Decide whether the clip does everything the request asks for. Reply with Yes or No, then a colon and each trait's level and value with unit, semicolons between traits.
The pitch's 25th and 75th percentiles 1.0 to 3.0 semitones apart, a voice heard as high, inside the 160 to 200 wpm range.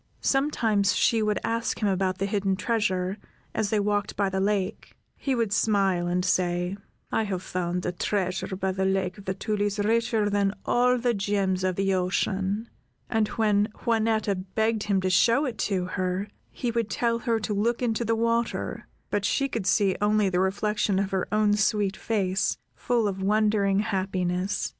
Yes: narrow, 2.6 semitones; high, 205 Hz; average, 180 wpm